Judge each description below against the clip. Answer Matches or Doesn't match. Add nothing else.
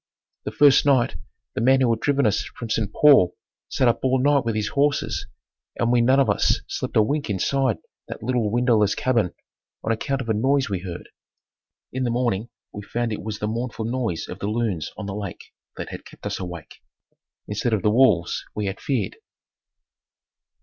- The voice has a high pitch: Doesn't match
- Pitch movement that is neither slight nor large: Matches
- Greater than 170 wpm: Matches